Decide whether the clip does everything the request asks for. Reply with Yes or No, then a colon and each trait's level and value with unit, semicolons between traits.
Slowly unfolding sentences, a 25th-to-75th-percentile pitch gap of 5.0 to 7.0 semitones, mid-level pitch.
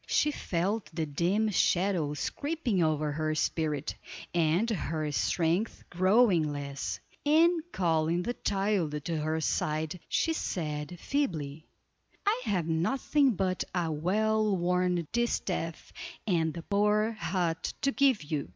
Yes: slow, 125 wpm; average, 5.3 semitones; medium, 175 Hz